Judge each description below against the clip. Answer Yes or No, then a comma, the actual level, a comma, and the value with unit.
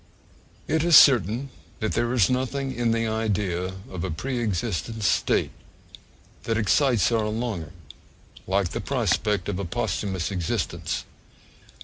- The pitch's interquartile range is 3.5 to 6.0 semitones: Yes, average, 4.3 semitones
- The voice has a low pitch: Yes, low, 110 Hz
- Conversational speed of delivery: No, slow, 130 wpm